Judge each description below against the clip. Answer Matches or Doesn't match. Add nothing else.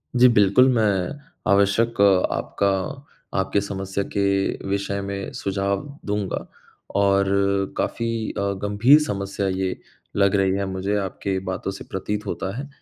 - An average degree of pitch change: Doesn't match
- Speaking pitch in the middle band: Doesn't match